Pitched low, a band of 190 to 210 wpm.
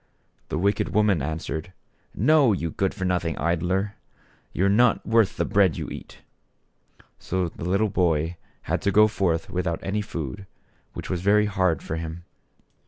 No: very low, 95 Hz; average, 165 wpm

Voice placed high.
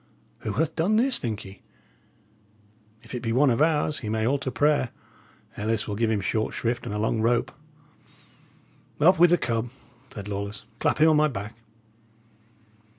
No: low, 120 Hz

